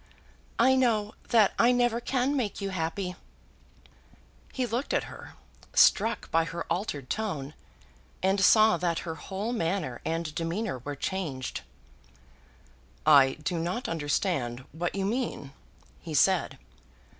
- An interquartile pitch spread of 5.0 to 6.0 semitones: Yes, wide, 5.4 semitones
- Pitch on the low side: No, medium, 185 Hz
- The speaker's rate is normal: No, slow, 130 wpm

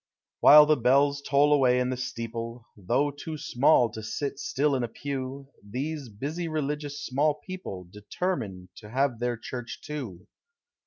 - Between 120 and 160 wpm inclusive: Yes, average, 155 wpm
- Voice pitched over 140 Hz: No, low, 130 Hz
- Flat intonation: No, average, 4.0 semitones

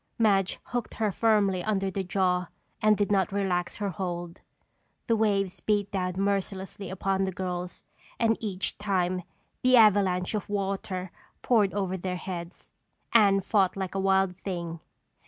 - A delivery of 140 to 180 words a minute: Yes, average, 150 wpm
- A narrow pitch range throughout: Yes, narrow, 1.9 semitones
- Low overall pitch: No, high, 195 Hz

